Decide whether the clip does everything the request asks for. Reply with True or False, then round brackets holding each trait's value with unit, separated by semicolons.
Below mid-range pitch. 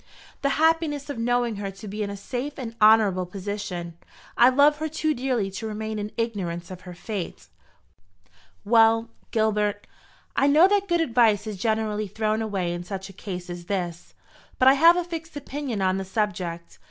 False (215 Hz)